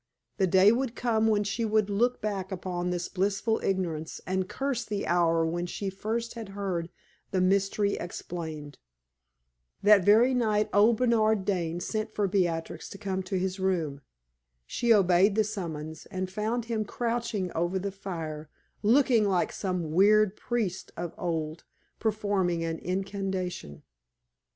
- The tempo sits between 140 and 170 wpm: Yes, average, 145 wpm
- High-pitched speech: Yes, high, 195 Hz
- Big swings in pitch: No, average, 3.4 semitones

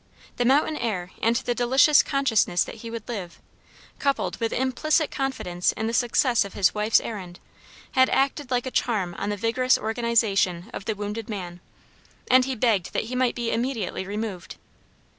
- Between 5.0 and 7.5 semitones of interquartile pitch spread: No, average, 4.0 semitones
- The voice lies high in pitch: Yes, high, 230 Hz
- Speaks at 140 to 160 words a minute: No, average, 175 wpm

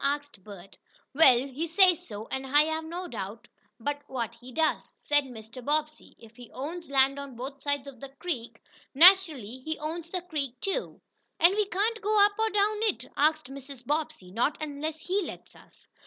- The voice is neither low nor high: No, very high, 290 Hz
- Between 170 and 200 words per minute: Yes, average, 185 wpm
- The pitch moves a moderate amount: Yes, average, 4.9 semitones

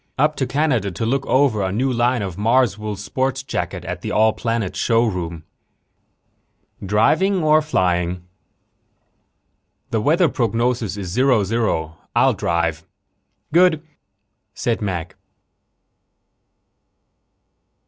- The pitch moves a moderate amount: No, wide, 5.7 semitones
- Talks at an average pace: No, slow, 105 wpm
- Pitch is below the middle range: Yes, low, 115 Hz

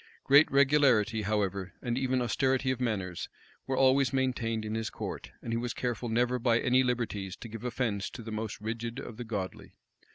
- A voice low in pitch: Yes, low, 120 Hz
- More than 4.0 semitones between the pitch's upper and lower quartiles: No, average, 3.0 semitones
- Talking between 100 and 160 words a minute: No, average, 190 wpm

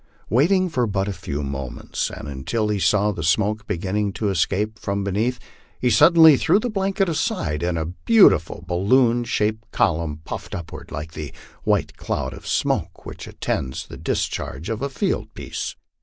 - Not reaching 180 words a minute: Yes, average, 170 wpm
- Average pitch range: No, wide, 7.1 semitones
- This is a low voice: Yes, low, 105 Hz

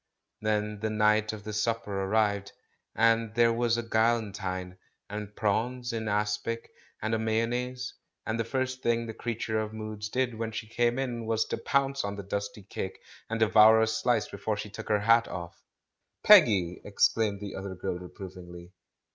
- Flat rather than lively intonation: Yes, narrow, 2.1 semitones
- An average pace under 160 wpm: No, average, 170 wpm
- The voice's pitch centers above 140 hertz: No, low, 110 Hz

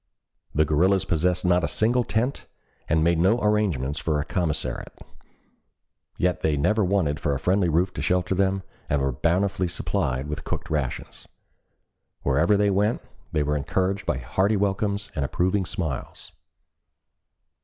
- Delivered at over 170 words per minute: No, average, 150 wpm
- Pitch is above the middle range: No, very low, 90 Hz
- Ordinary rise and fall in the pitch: Yes, average, 4.8 semitones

